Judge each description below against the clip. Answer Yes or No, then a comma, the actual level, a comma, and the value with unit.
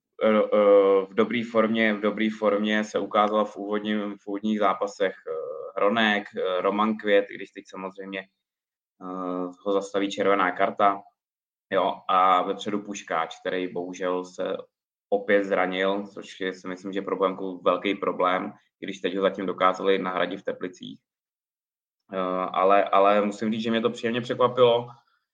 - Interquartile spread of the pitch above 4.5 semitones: No, narrow, 2.5 semitones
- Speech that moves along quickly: No, average, 135 wpm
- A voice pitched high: No, low, 100 Hz